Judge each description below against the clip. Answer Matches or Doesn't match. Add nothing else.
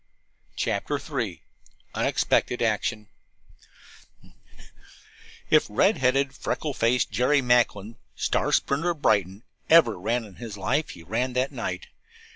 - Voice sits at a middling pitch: Doesn't match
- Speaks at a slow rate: Matches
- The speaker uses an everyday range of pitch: Matches